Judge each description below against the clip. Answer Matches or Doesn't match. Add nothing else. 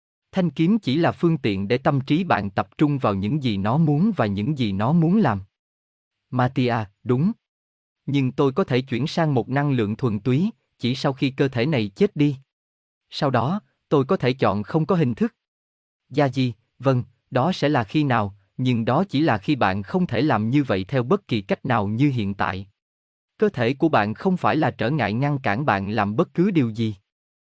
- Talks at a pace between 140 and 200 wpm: Doesn't match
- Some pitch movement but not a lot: Doesn't match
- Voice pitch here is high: Doesn't match